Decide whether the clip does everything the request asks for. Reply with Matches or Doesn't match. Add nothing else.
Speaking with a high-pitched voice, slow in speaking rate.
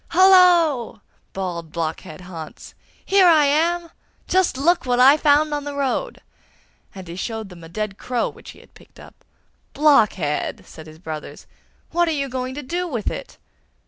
Doesn't match